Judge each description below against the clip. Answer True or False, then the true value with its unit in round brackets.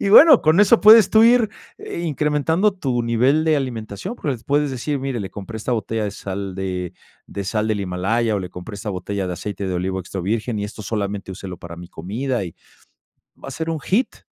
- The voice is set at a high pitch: False (110 Hz)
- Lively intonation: True (7.3 semitones)